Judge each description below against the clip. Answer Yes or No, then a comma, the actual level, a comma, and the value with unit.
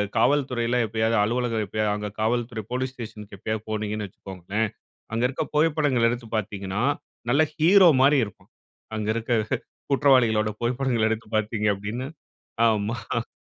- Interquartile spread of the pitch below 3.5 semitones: Yes, average, 2.9 semitones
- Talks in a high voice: No, low, 115 Hz